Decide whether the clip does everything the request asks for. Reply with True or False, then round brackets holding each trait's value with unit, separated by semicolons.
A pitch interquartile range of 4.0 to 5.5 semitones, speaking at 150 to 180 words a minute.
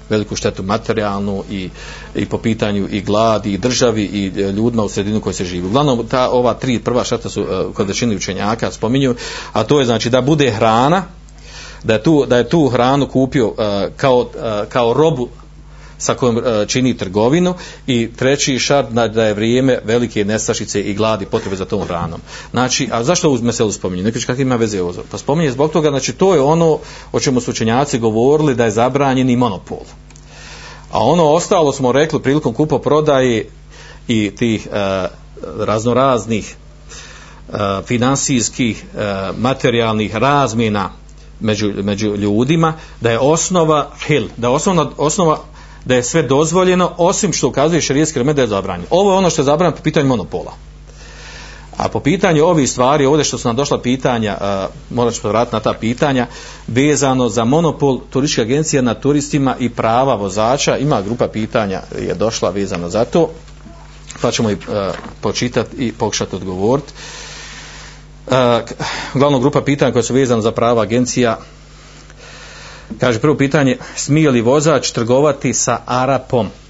True (4.5 semitones; 160 wpm)